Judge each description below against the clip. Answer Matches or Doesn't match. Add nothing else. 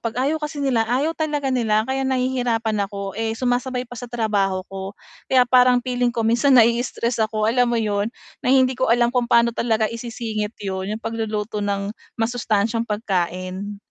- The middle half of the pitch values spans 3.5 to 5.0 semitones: Doesn't match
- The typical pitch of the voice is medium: Doesn't match